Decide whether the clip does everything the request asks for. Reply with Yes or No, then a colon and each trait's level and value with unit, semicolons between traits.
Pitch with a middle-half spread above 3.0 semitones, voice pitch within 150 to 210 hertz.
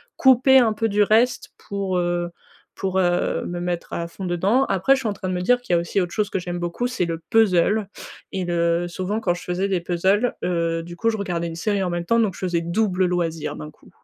Yes: average, 3.5 semitones; medium, 185 Hz